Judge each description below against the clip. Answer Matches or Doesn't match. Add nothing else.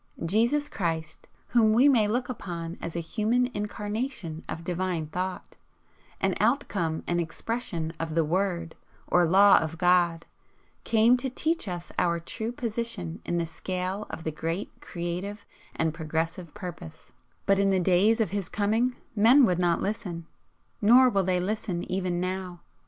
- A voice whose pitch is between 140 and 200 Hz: Matches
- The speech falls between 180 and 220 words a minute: Doesn't match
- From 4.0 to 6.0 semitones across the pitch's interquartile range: Matches